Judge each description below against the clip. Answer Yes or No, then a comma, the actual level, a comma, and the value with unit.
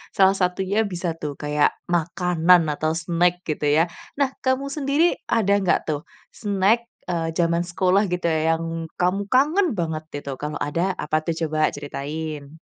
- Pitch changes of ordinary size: Yes, average, 3.9 semitones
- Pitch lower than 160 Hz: No, medium, 170 Hz